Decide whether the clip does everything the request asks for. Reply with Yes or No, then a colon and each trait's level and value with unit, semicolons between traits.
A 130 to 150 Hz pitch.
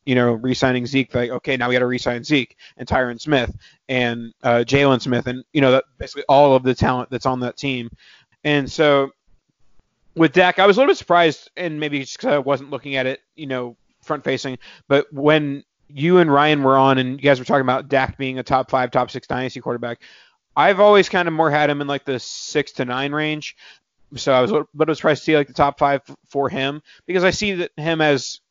Yes: low, 135 Hz